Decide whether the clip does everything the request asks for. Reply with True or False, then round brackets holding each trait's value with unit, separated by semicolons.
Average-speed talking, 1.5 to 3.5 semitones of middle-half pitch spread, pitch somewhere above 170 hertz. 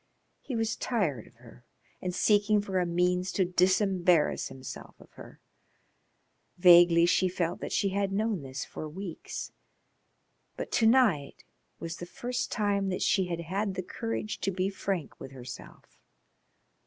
True (150 wpm; 3.1 semitones; 185 Hz)